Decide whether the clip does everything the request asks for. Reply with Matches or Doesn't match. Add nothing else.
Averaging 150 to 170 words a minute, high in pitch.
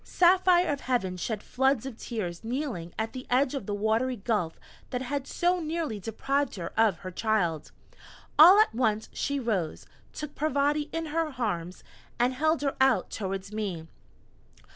Matches